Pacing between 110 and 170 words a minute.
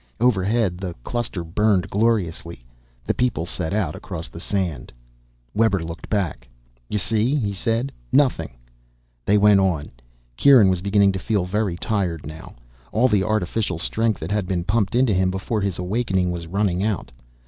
Yes: average, 160 wpm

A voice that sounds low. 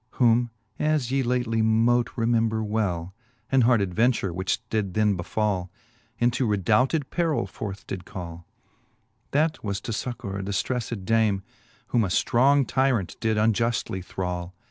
Yes: low, 110 Hz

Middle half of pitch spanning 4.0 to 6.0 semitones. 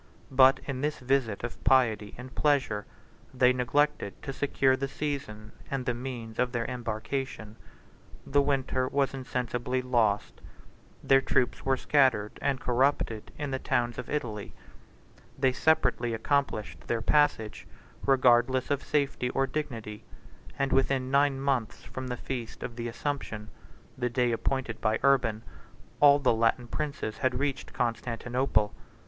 No: average, 2.8 semitones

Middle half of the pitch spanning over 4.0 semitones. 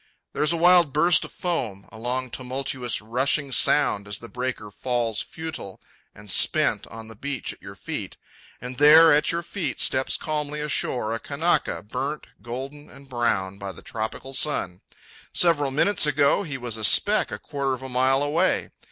Yes: average, 4.4 semitones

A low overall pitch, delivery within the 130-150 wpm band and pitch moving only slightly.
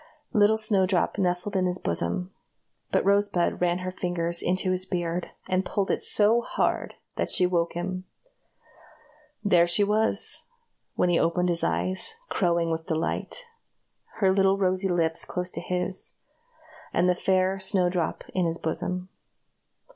No: medium, 180 Hz; average, 145 wpm; narrow, 1.7 semitones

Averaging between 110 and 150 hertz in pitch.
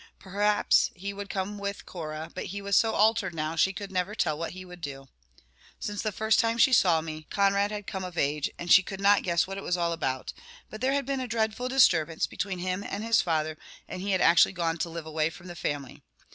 No: medium, 185 Hz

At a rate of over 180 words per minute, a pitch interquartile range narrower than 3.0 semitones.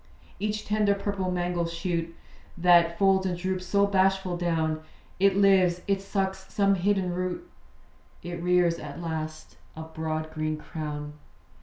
No: average, 140 wpm; narrow, 2.6 semitones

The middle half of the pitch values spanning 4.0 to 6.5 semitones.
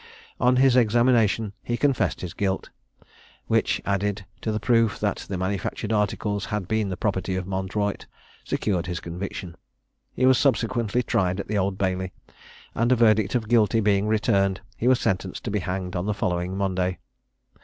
No: average, 3.1 semitones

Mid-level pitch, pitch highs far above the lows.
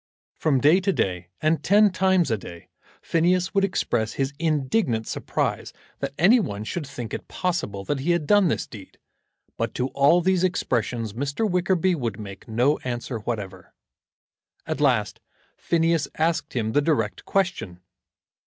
Yes: medium, 145 Hz; wide, 7.9 semitones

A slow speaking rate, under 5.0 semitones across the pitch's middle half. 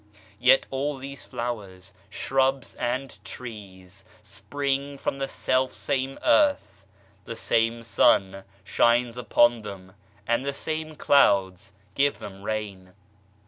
No: slow, 115 wpm; wide, 5.5 semitones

